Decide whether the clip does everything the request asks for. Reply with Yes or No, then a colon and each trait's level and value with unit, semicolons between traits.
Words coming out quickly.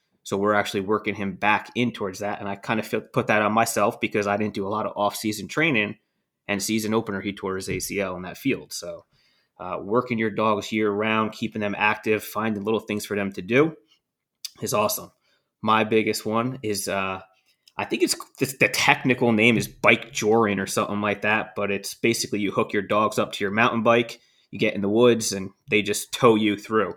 Yes: fast, 215 wpm